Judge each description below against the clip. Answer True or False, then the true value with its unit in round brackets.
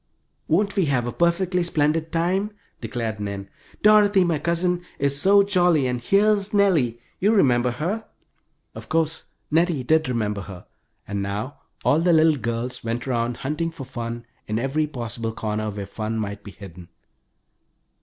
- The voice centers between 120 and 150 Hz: True (140 Hz)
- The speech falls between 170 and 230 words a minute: False (155 wpm)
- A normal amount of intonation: False (7.1 semitones)